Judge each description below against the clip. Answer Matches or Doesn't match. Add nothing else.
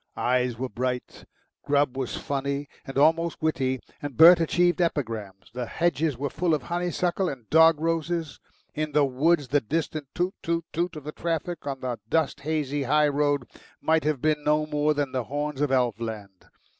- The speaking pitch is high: Doesn't match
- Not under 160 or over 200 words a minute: Matches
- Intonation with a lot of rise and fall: Doesn't match